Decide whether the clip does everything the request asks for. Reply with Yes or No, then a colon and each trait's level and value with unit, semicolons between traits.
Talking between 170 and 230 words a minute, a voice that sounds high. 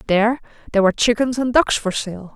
Yes: fast, 205 wpm; high, 225 Hz